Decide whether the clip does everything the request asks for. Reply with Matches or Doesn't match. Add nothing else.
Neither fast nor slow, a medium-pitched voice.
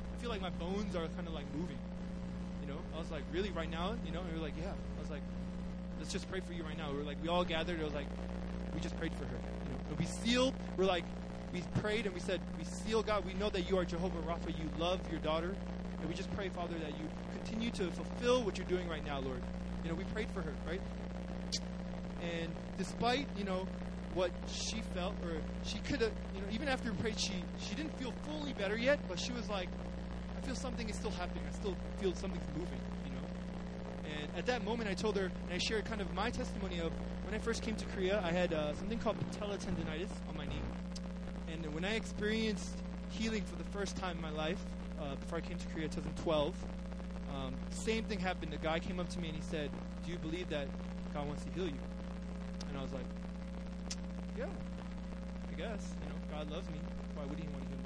Doesn't match